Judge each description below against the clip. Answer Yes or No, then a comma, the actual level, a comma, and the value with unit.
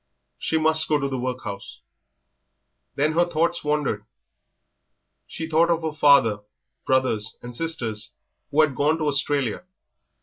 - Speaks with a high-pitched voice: No, medium, 145 Hz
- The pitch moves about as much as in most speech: Yes, average, 4.0 semitones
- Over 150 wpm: No, slow, 135 wpm